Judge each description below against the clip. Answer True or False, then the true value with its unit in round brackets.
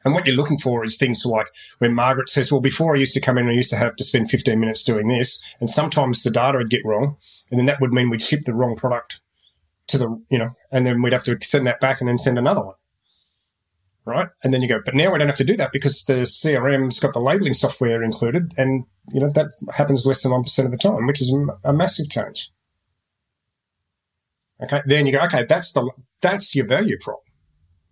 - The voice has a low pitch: True (130 Hz)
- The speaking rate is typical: False (235 wpm)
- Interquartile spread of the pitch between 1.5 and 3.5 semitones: True (2.9 semitones)